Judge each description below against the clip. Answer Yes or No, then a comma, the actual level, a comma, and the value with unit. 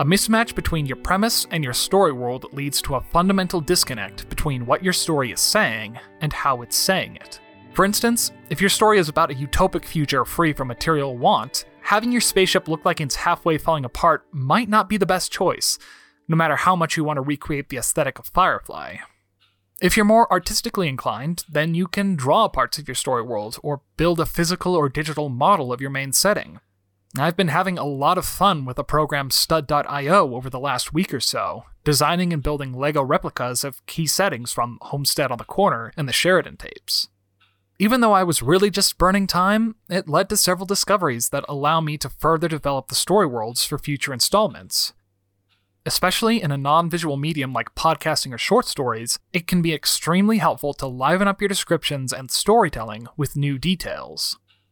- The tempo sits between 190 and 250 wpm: Yes, average, 195 wpm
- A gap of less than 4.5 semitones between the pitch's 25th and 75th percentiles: No, wide, 5.4 semitones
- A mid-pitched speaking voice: Yes, medium, 155 Hz